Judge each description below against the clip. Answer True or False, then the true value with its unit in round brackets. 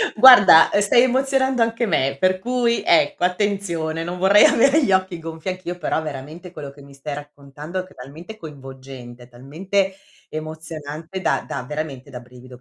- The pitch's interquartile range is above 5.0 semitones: True (5.5 semitones)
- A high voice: False (165 Hz)